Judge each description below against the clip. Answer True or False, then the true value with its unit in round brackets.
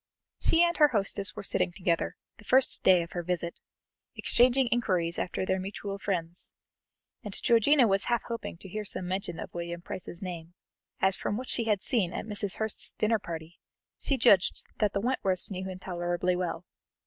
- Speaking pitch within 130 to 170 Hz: False (190 Hz)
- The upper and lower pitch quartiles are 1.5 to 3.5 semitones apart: False (3.9 semitones)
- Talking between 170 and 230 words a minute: True (185 wpm)